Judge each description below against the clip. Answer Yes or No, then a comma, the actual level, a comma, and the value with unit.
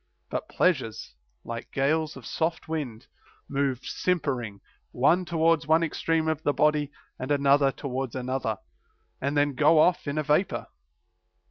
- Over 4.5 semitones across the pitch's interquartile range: No, average, 3.1 semitones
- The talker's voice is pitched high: No, medium, 145 Hz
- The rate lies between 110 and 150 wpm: Yes, average, 140 wpm